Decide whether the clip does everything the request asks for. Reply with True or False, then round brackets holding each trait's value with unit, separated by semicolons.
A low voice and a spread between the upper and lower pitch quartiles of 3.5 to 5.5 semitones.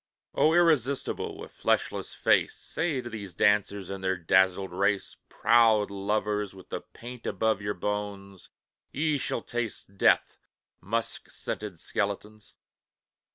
False (105 Hz; 2.9 semitones)